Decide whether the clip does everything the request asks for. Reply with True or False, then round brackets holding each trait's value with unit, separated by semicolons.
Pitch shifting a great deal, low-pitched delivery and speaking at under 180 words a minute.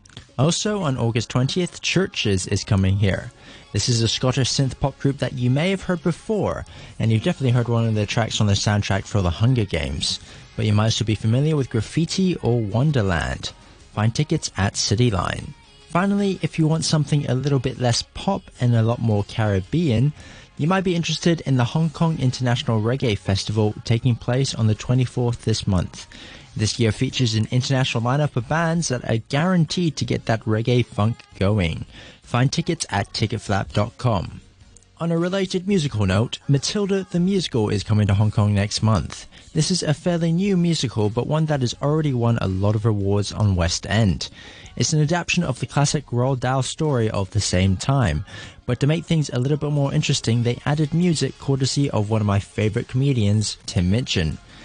False (5.7 semitones; 120 Hz; 190 wpm)